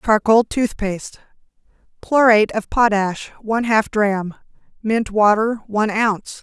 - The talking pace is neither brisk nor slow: No, slow, 110 wpm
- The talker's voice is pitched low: No, high, 215 Hz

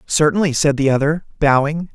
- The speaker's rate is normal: Yes, average, 155 wpm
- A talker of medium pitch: Yes, medium, 150 Hz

